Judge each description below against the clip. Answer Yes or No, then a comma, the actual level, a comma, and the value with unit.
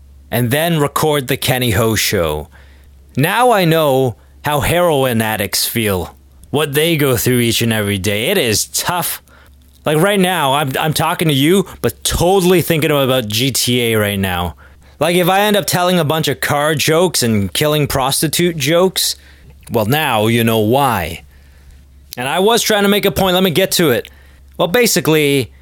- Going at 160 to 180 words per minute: Yes, average, 175 wpm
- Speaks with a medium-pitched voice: No, low, 130 Hz